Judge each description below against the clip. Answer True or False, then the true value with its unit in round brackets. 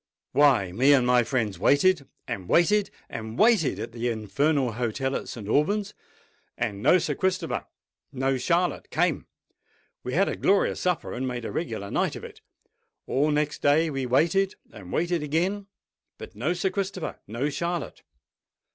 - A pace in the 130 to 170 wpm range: True (145 wpm)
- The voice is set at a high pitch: False (145 Hz)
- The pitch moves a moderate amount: False (6.6 semitones)